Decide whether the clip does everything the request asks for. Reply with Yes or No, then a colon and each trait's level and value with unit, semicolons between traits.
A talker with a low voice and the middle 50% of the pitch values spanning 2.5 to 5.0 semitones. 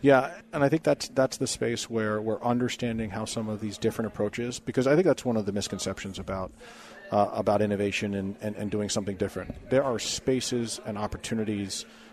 Yes: low, 110 Hz; average, 2.8 semitones